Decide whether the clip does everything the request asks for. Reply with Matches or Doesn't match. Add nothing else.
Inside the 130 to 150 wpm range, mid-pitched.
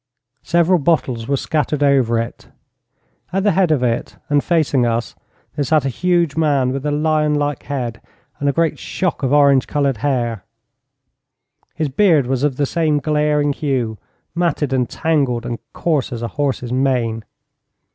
Doesn't match